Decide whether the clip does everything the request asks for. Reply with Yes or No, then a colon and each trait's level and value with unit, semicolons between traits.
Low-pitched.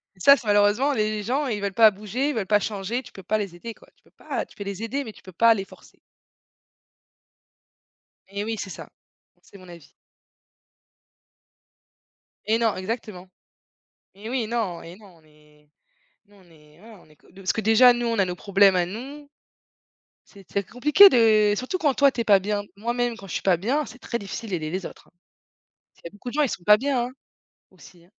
No: high, 210 Hz